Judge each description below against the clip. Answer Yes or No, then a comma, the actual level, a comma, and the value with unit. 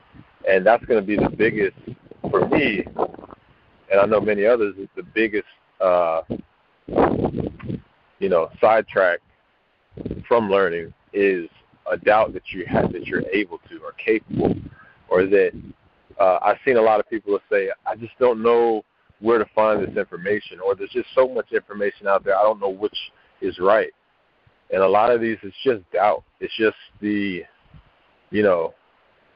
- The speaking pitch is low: No, very high, 325 Hz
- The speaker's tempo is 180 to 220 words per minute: No, average, 165 wpm